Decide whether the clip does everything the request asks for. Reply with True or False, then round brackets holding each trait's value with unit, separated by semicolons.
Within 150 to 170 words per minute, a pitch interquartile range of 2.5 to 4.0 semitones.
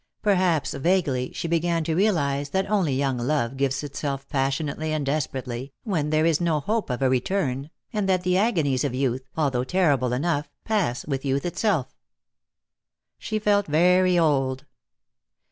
False (155 wpm; 5.1 semitones)